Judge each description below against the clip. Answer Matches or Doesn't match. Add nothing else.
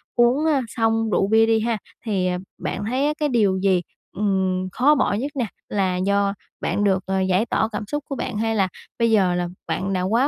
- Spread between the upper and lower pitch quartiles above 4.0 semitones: Doesn't match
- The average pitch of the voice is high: Matches